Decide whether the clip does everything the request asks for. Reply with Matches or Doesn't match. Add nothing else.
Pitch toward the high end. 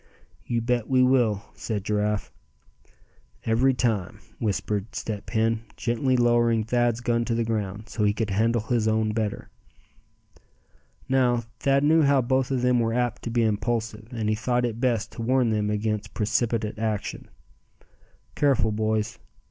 Doesn't match